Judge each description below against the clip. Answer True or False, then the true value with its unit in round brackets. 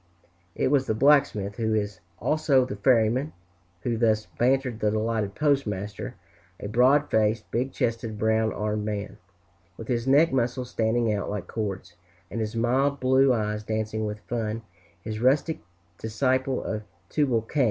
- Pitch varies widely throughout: False (3.4 semitones)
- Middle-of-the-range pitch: False (115 Hz)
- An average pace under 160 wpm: True (150 wpm)